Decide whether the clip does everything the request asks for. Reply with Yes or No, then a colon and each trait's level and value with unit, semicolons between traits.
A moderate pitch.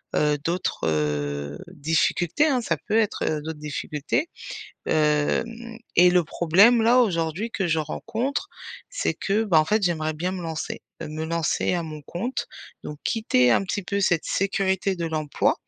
Yes: medium, 170 Hz